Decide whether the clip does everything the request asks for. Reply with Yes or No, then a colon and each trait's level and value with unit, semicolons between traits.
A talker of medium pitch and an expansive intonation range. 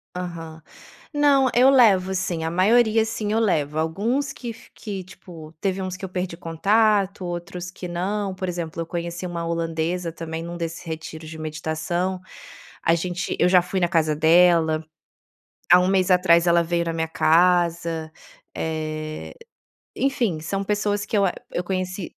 No: medium, 175 Hz; average, 2.8 semitones